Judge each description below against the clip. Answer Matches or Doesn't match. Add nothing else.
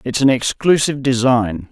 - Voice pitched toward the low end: Matches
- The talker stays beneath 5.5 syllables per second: Matches